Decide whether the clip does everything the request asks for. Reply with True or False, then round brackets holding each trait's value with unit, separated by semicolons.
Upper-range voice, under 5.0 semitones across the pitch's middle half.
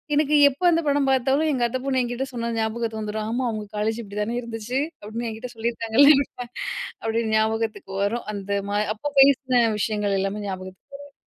True (230 Hz; 3.4 semitones)